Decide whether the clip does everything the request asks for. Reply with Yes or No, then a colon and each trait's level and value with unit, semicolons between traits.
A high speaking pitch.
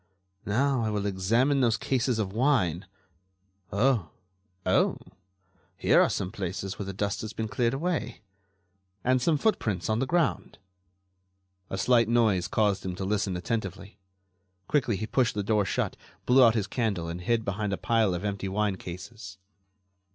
No: low, 105 Hz